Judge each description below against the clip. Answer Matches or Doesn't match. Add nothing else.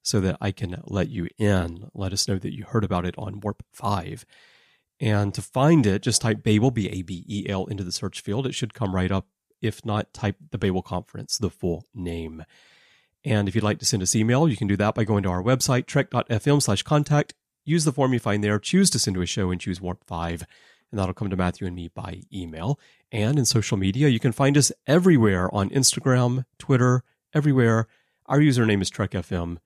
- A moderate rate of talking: Doesn't match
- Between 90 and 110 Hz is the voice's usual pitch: Matches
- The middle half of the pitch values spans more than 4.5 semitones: Matches